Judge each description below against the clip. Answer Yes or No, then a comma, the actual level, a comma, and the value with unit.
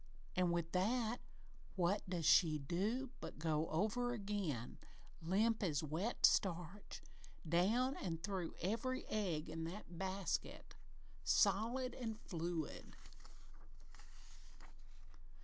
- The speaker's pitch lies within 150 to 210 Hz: Yes, high, 190 Hz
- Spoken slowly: Yes, slow, 100 wpm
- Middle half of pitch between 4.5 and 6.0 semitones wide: Yes, average, 4.8 semitones